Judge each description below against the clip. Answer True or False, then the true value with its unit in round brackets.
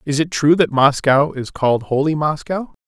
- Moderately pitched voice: True (145 Hz)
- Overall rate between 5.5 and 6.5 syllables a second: False (4.9 syllables/s)